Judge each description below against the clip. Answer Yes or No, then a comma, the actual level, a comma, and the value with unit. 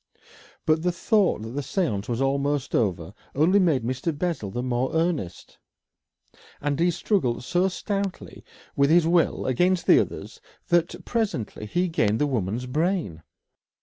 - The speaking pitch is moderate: Yes, medium, 145 Hz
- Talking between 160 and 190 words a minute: No, average, 150 wpm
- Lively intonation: Yes, wide, 6.4 semitones